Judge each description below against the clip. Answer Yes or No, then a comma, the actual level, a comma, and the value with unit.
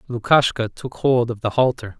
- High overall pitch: No, low, 120 Hz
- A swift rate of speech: No, average, 180 wpm